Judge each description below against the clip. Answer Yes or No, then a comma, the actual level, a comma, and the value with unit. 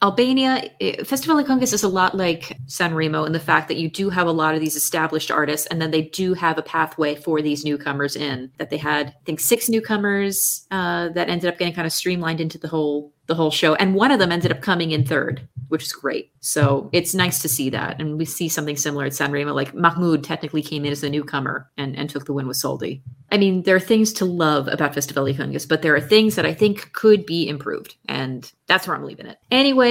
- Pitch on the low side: No, medium, 160 Hz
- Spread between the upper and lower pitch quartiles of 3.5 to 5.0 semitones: Yes, average, 4.0 semitones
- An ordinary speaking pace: No, fast, 245 wpm